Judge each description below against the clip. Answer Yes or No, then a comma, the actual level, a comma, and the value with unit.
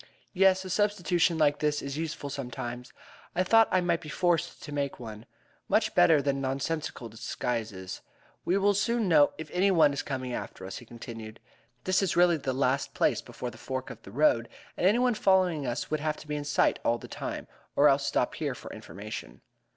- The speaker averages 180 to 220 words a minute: Yes, average, 200 wpm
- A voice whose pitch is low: No, medium, 145 Hz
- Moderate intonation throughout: No, wide, 6.3 semitones